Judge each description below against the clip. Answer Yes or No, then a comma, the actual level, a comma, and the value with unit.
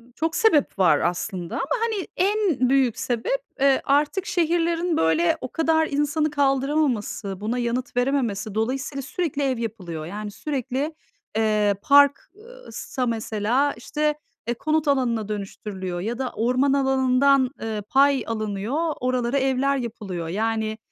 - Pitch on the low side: No, very high, 255 Hz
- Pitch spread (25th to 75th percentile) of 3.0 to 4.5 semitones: No, average, 5.0 semitones